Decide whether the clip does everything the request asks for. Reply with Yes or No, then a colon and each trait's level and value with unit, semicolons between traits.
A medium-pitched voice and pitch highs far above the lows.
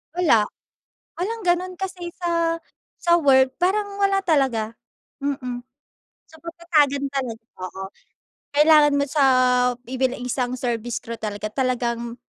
No: very high, 280 Hz; wide, 5.9 semitones